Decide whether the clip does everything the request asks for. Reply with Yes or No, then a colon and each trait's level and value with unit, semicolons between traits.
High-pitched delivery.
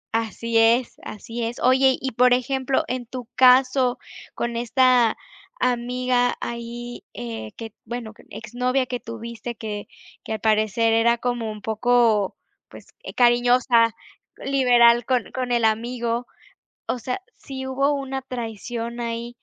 Yes: high, 240 Hz